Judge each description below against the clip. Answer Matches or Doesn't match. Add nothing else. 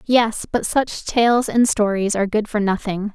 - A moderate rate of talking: Matches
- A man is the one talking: Doesn't match